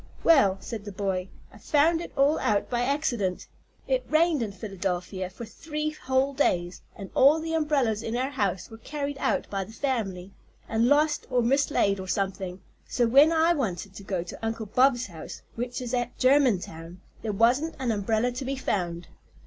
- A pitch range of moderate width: No, wide, 6.2 semitones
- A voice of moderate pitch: No, high, 235 Hz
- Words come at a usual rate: Yes, average, 185 wpm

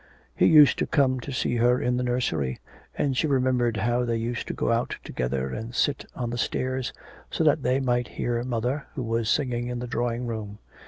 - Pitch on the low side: Yes, low, 120 Hz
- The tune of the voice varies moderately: No, narrow, 1.7 semitones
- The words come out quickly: Yes, fast, 210 wpm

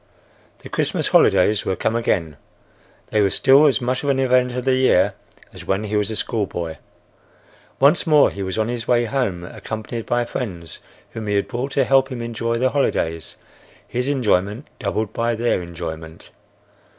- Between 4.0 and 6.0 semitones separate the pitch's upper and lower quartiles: Yes, average, 4.5 semitones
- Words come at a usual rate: Yes, average, 175 wpm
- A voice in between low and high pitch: No, low, 115 Hz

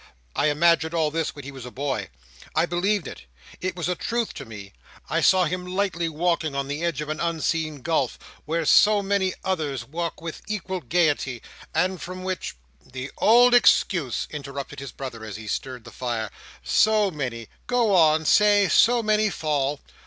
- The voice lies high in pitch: No, medium, 165 Hz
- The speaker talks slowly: No, average, 180 wpm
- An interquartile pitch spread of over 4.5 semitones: Yes, average, 5.2 semitones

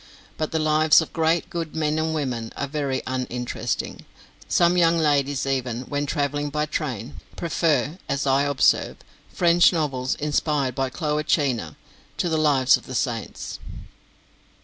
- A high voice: No, medium, 145 Hz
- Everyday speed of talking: Yes, average, 150 wpm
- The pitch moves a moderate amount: Yes, average, 3.1 semitones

